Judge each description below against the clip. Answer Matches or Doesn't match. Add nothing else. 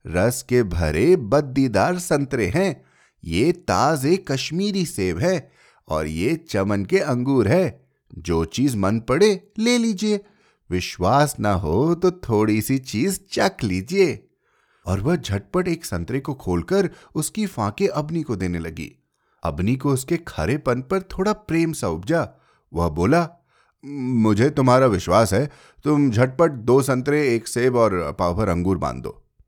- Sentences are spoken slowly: Doesn't match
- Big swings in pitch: Matches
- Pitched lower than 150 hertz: Matches